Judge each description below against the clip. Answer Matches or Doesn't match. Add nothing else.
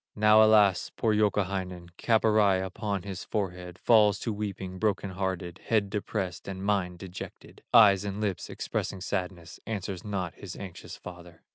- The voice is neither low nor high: Doesn't match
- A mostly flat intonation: Matches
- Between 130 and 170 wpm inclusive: Matches